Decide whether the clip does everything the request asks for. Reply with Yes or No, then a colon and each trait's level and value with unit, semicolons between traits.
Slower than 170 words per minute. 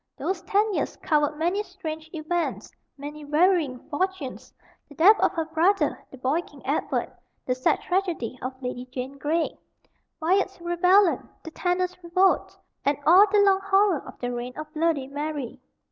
Yes: average, 160 wpm